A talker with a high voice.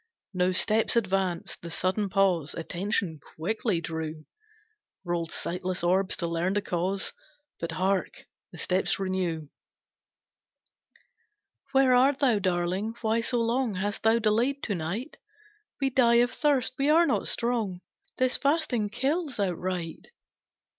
Yes: high, 195 Hz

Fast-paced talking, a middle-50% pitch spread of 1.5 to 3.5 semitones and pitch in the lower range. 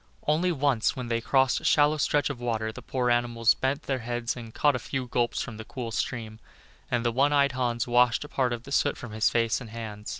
Yes: fast, 240 wpm; narrow, 2.6 semitones; low, 120 Hz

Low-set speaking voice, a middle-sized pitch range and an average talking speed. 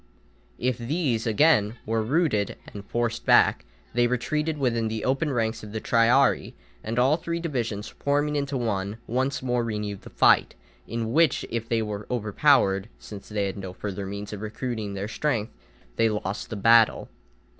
Yes: low, 115 Hz; average, 3.8 semitones; average, 165 wpm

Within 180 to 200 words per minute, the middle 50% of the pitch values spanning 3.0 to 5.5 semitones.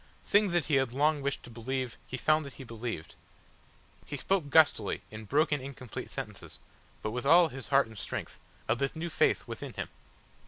Yes: average, 190 wpm; average, 4.4 semitones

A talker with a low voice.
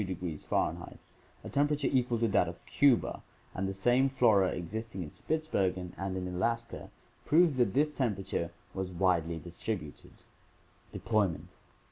Yes: low, 100 Hz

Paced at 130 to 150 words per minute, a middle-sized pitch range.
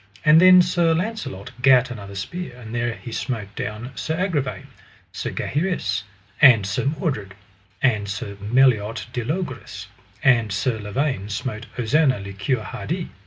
No: average, 145 wpm; wide, 6.6 semitones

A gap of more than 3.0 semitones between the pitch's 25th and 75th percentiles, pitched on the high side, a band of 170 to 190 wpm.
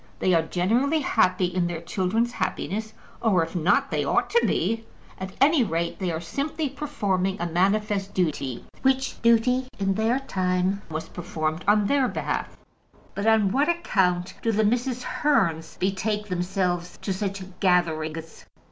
No: average, 4.6 semitones; high, 195 Hz; average, 155 wpm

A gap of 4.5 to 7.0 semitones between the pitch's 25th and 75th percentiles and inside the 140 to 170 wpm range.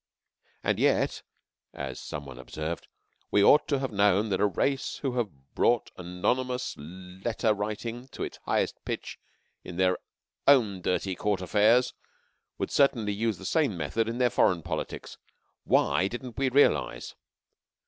Yes: average, 5.2 semitones; average, 150 wpm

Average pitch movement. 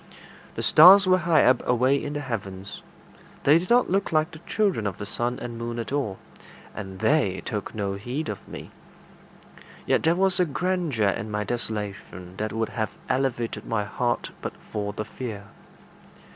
No: wide, 6.8 semitones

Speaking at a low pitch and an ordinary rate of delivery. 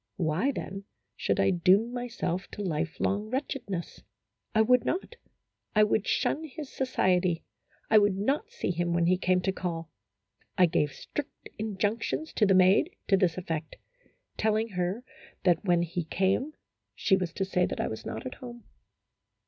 No: high, 195 Hz; average, 165 wpm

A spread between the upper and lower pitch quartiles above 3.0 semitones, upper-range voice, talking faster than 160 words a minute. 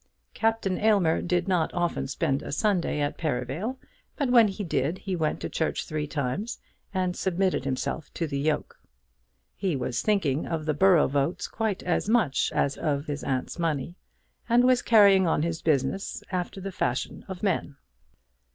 No: average, 5.1 semitones; medium, 170 Hz; average, 170 wpm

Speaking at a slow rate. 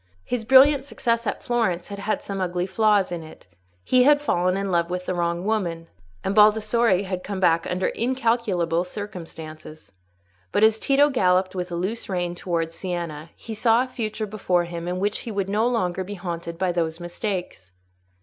No: average, 185 wpm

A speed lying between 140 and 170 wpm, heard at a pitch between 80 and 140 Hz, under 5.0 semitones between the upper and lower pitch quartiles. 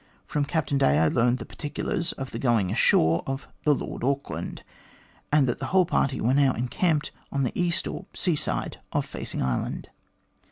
No: average, 185 wpm; low, 135 Hz; average, 3.9 semitones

